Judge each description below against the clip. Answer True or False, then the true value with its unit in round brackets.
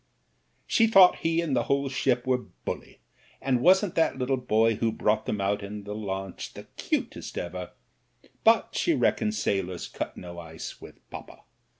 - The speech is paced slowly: False (170 wpm)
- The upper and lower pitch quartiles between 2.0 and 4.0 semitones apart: False (5.5 semitones)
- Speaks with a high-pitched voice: False (110 Hz)